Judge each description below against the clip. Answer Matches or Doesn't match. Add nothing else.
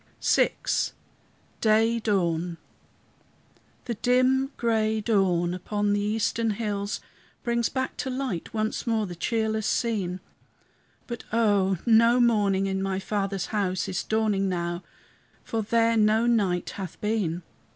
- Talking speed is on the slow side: Matches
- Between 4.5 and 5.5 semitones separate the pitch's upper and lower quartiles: Doesn't match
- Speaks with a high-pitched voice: Matches